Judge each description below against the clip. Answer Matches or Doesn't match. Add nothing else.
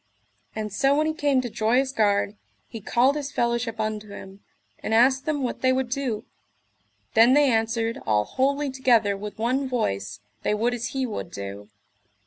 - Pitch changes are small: Doesn't match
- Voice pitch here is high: Matches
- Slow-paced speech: Doesn't match